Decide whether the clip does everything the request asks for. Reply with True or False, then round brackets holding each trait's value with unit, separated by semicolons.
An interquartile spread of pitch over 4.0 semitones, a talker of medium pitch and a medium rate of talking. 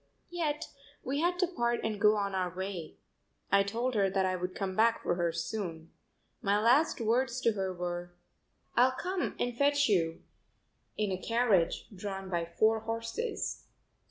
False (4.7 semitones; 210 Hz; 165 wpm)